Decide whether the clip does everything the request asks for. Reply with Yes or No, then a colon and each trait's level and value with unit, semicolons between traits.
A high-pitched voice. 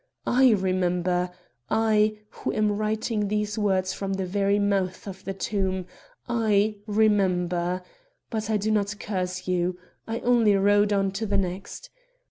Yes: high, 200 Hz